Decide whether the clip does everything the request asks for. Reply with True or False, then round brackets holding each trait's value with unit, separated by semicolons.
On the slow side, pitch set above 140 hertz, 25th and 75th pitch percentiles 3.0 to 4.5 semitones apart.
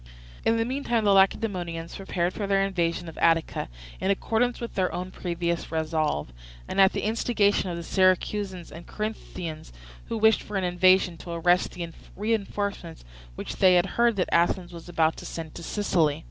False (175 wpm; 185 Hz; 3.3 semitones)